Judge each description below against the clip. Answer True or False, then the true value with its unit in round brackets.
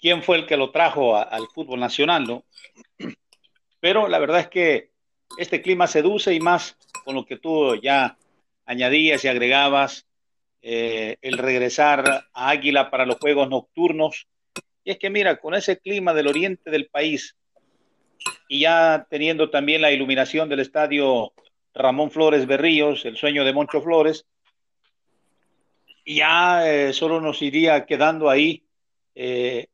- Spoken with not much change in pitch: False (3.3 semitones)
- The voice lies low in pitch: False (150 Hz)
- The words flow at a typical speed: True (145 wpm)